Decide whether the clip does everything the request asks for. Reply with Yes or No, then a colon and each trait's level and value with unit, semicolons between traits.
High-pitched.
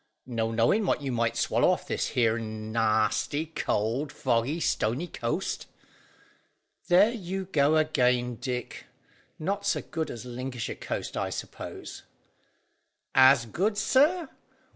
No: low, 130 Hz